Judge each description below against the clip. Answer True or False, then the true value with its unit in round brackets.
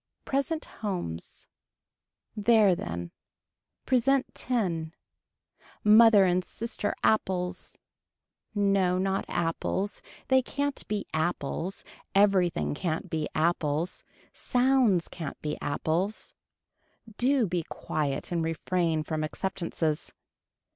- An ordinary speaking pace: False (90 wpm)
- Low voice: False (185 Hz)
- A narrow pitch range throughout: False (4.9 semitones)